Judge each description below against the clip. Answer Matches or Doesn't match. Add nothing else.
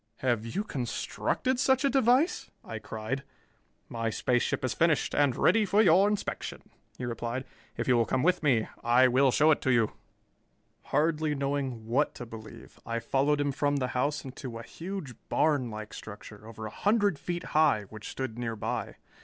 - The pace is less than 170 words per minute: Doesn't match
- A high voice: Doesn't match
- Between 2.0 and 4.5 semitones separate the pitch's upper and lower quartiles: Doesn't match